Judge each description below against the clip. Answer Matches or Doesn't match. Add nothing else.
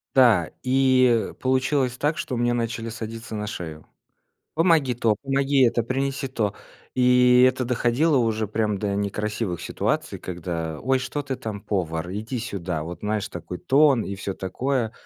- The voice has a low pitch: Matches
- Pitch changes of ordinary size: Matches